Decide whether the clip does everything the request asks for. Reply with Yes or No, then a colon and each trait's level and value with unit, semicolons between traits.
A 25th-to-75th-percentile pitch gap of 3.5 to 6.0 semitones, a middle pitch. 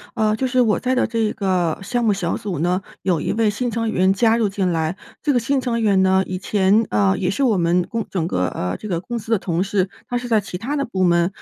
No: average, 4.1 semitones; high, 200 Hz